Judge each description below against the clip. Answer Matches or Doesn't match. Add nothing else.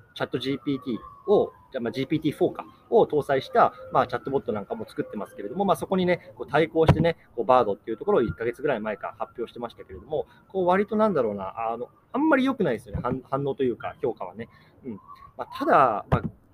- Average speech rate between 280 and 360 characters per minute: Doesn't match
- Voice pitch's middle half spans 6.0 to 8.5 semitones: Matches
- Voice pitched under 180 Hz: Matches